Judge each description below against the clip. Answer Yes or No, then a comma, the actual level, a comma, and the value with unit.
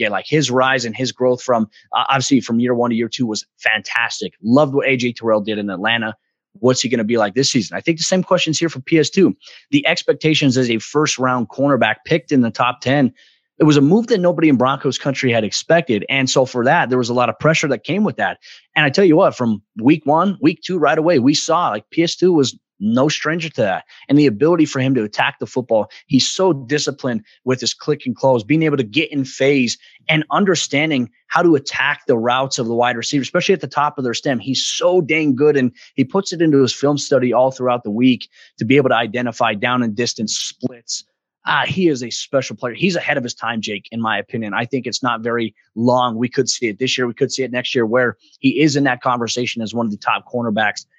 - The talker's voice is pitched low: Yes, low, 130 Hz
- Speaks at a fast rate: Yes, fast, 245 wpm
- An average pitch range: Yes, average, 3.8 semitones